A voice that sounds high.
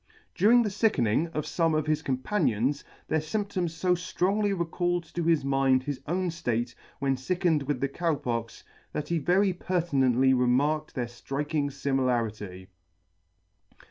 No: medium, 150 Hz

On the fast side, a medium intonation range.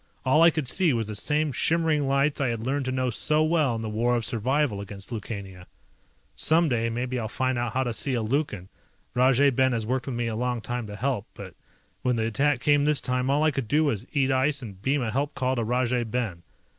Yes: fast, 235 wpm; average, 3.7 semitones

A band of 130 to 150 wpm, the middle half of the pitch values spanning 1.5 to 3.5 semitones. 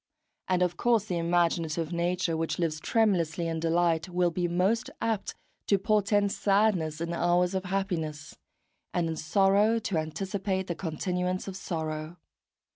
Yes: average, 145 wpm; average, 2.9 semitones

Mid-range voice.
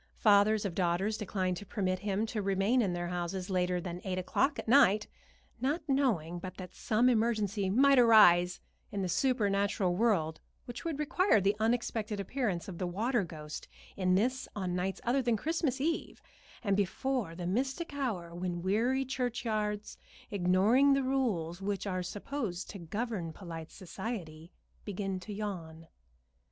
No: high, 200 Hz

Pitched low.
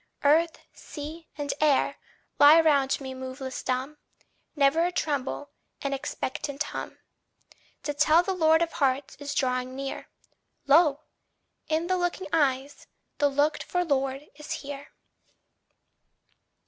No: very high, 290 Hz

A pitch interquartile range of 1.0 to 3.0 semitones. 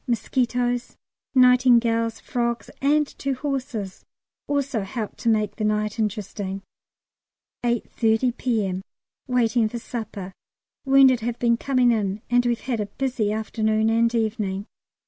Yes: narrow, 2.6 semitones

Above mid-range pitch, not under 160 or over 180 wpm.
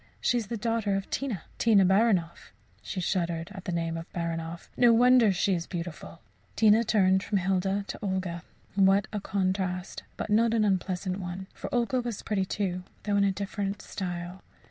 Yes: high, 195 Hz; average, 175 wpm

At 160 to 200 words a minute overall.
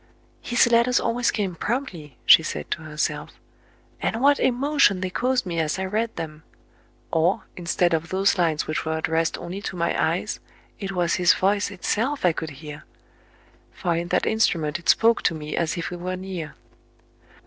Yes: average, 185 wpm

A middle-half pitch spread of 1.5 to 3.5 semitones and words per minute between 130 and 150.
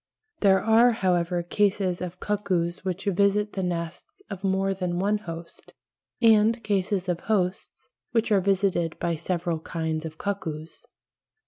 Yes: average, 2.9 semitones; average, 140 wpm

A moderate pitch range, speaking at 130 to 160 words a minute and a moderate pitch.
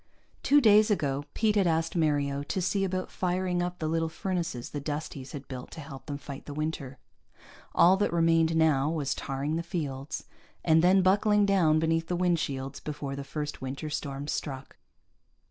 No: average, 4.0 semitones; average, 180 wpm; medium, 160 Hz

